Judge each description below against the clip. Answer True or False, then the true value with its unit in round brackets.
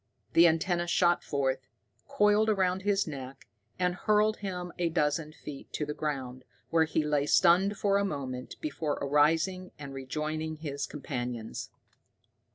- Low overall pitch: False (155 Hz)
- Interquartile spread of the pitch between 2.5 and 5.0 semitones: True (4.5 semitones)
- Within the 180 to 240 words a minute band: False (145 wpm)